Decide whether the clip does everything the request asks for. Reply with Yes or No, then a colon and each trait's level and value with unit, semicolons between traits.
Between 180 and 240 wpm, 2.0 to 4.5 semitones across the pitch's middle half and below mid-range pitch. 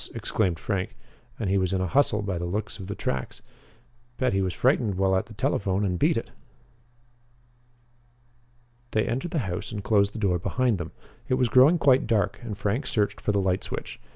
Yes: average, 200 wpm; average, 3.8 semitones; low, 100 Hz